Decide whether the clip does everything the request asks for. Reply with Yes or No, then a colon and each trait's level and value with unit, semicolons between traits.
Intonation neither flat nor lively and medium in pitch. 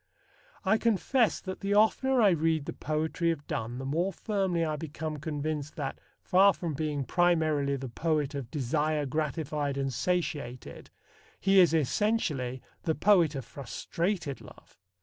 Yes: average, 4.2 semitones; medium, 155 Hz